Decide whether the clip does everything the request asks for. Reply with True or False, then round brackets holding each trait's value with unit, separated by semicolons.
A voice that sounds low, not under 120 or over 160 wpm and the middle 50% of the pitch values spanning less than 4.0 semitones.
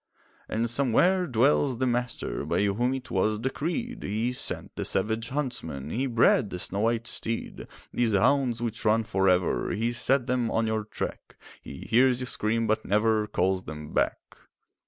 False (115 Hz; 170 wpm; 2.9 semitones)